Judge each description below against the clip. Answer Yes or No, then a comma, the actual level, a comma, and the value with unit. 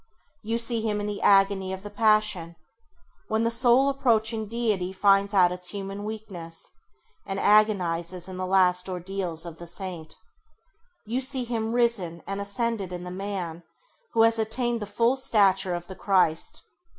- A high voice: Yes, high, 200 Hz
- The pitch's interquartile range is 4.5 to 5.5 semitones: No, average, 3.6 semitones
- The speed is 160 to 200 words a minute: Yes, average, 165 wpm